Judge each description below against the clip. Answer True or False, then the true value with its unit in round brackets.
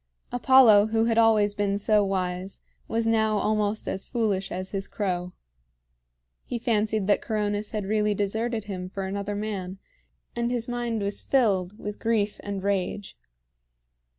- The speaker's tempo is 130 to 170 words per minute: True (150 wpm)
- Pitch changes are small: True (2.2 semitones)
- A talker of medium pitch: False (210 Hz)